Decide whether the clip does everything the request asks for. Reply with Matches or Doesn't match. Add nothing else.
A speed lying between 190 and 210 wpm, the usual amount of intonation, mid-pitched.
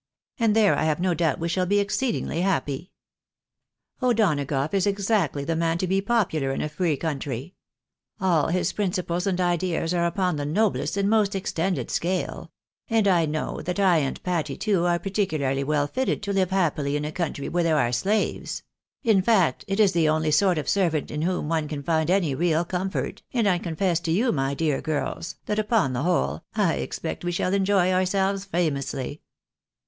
Matches